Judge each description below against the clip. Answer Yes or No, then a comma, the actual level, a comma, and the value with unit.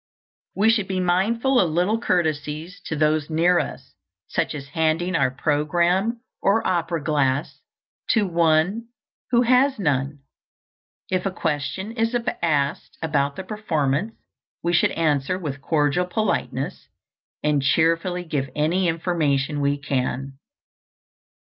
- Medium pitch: Yes, medium, 165 Hz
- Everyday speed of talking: No, slow, 125 wpm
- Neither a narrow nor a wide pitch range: Yes, average, 4.3 semitones